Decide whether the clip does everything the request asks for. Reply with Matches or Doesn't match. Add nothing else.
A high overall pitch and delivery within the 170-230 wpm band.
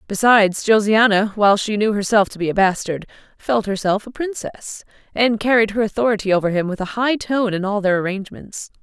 Matches